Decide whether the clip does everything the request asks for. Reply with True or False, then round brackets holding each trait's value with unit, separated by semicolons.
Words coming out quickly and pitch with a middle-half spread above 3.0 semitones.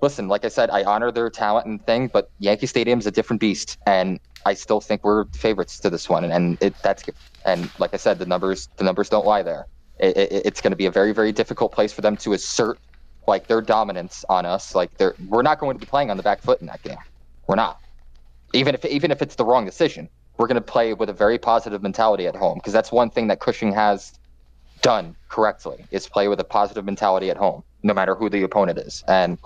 True (250 wpm; 4.1 semitones)